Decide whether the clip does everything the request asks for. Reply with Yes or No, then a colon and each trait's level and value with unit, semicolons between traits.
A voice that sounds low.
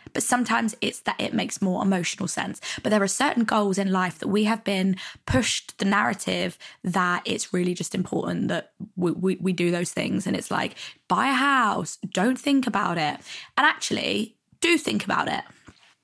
No: high, 195 Hz